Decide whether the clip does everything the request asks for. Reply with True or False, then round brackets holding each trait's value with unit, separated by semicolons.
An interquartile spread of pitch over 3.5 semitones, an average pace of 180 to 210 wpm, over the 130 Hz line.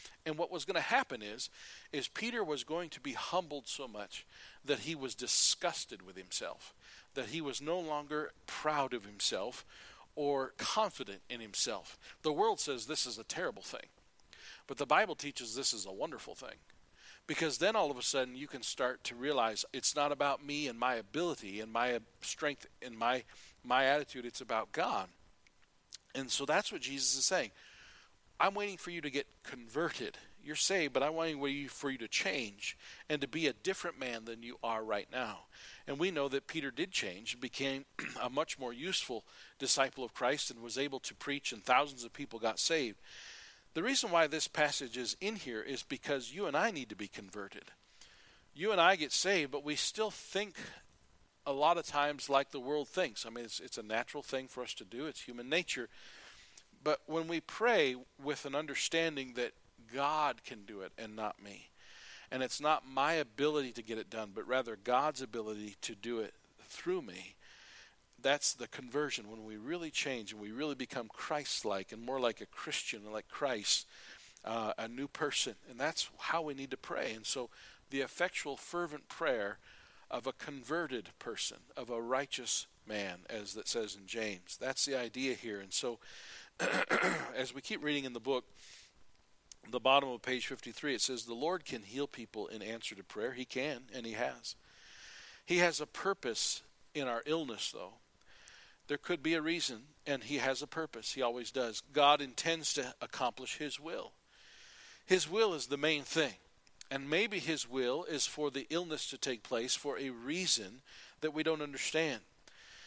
True (4.2 semitones; 190 wpm; 140 Hz)